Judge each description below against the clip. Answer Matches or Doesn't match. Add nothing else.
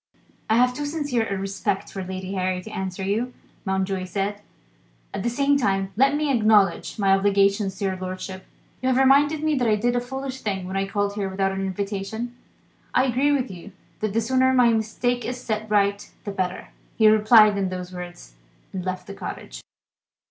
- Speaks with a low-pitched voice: Doesn't match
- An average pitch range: Matches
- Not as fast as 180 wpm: Doesn't match